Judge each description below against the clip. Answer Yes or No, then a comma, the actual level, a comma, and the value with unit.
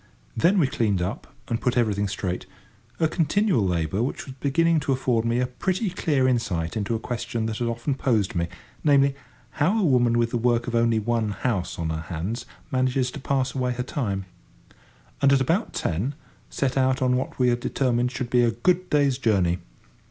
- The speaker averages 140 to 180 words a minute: No, average, 195 wpm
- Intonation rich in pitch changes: No, average, 3.6 semitones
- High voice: No, low, 125 Hz